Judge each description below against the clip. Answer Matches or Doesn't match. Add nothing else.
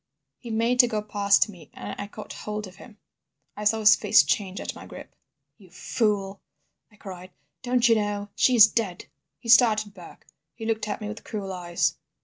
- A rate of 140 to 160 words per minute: Doesn't match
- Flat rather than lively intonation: Matches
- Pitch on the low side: Doesn't match